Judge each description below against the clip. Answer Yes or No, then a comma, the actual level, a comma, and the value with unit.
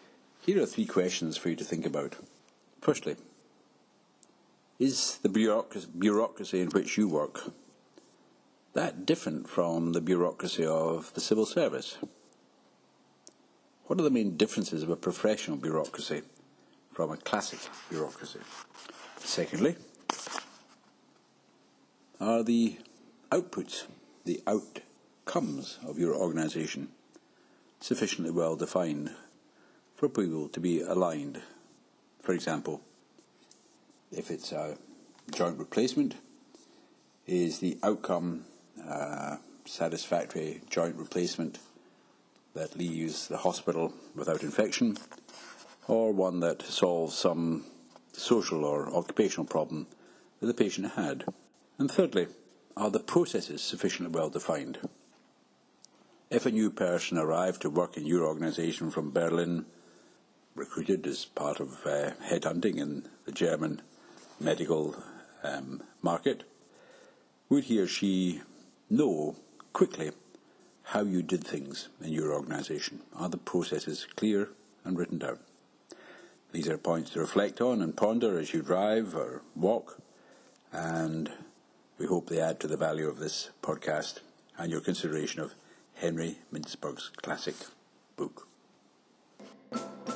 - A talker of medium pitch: No, very low, 85 Hz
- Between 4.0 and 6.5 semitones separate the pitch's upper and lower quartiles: Yes, average, 4.4 semitones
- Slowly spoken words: Yes, slow, 115 wpm